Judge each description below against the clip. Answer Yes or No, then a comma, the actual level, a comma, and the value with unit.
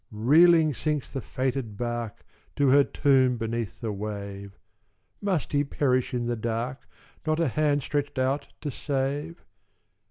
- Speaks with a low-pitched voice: Yes, low, 130 Hz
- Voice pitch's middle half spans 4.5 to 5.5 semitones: No, average, 3.8 semitones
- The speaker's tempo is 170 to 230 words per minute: No, average, 140 wpm